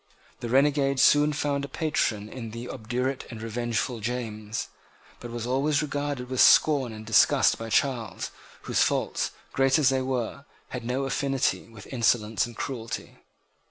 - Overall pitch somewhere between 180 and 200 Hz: No, low, 125 Hz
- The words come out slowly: No, average, 155 wpm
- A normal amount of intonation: Yes, average, 3.2 semitones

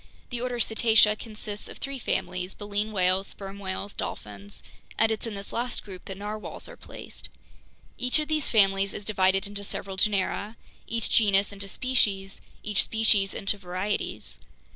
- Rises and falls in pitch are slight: Yes, narrow, 2.3 semitones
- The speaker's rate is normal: Yes, average, 160 wpm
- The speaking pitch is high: Yes, high, 205 Hz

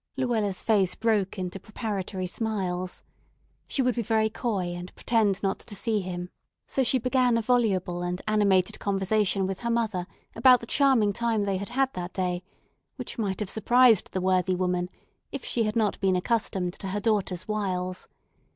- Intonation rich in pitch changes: No, average, 3.7 semitones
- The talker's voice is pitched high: Yes, high, 205 Hz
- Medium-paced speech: Yes, average, 175 wpm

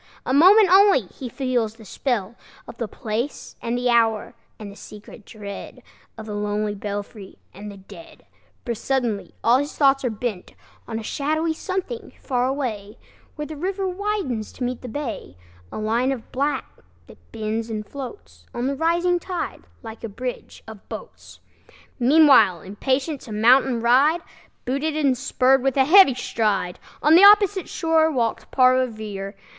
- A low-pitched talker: No, very high, 250 Hz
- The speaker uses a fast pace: No, average, 165 wpm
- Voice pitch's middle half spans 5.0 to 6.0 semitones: Yes, average, 5.3 semitones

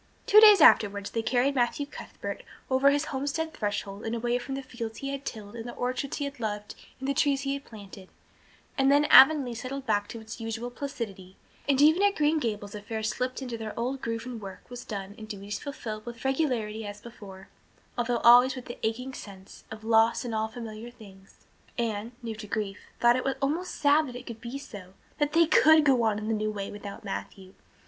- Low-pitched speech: No, high, 235 Hz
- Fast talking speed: Yes, fast, 210 wpm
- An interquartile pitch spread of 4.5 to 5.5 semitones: No, average, 4.1 semitones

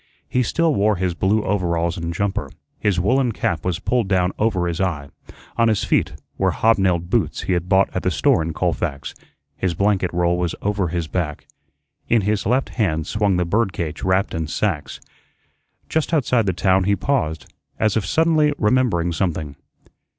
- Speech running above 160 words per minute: Yes, average, 180 wpm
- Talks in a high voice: No, very low, 95 Hz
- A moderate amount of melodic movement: Yes, average, 4.1 semitones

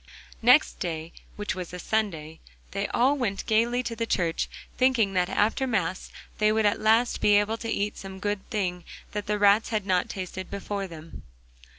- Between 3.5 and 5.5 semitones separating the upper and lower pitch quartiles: No, average, 3.0 semitones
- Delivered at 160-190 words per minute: Yes, average, 180 wpm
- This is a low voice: No, high, 205 Hz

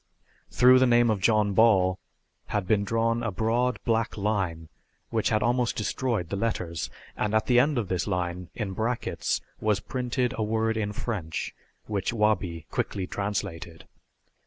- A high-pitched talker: No, low, 110 Hz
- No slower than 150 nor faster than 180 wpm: Yes, average, 160 wpm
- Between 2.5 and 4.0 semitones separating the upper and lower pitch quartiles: Yes, average, 3.6 semitones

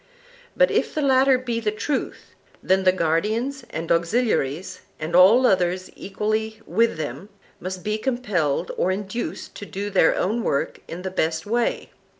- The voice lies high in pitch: Yes, high, 200 Hz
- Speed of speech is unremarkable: Yes, average, 155 wpm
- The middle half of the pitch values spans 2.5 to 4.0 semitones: No, average, 4.9 semitones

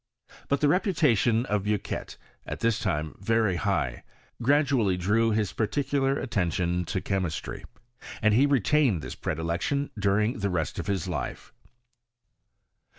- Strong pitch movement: Yes, wide, 6.5 semitones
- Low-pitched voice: Yes, low, 105 Hz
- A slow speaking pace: Yes, slow, 130 wpm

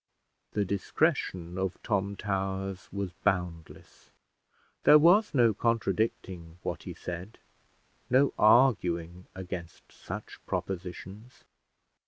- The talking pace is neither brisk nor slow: No, slow, 95 wpm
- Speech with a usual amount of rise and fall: Yes, average, 3.8 semitones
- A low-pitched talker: Yes, very low, 95 Hz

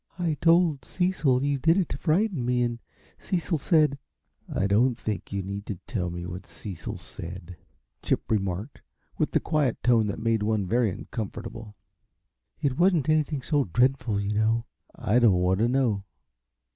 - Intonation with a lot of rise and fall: Yes, wide, 6.3 semitones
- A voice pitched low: Yes, low, 120 Hz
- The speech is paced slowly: No, average, 170 wpm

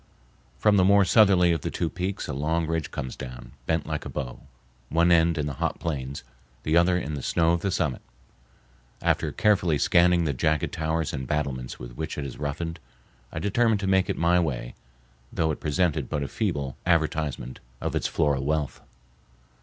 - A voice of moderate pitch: No, very low, 80 Hz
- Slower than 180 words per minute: No, average, 190 wpm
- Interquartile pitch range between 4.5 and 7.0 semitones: No, average, 3.5 semitones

